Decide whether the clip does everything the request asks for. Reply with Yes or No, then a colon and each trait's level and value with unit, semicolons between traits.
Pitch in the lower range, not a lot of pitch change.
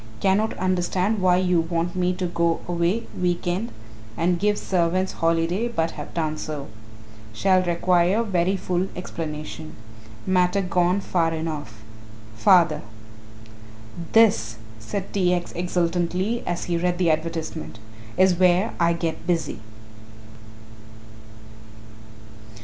No: medium, 175 Hz; narrow, 2.0 semitones